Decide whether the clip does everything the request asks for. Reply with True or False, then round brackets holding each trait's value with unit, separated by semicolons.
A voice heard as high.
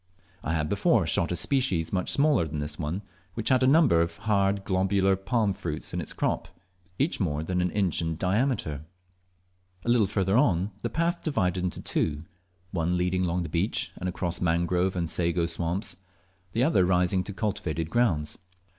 False (90 Hz)